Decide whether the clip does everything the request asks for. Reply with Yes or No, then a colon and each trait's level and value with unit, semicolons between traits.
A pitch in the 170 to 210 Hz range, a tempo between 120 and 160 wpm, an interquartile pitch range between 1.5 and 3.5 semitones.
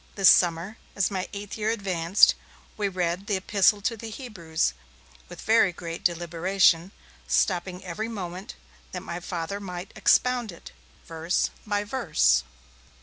Yes: high, 190 Hz; average, 140 wpm; average, 3.2 semitones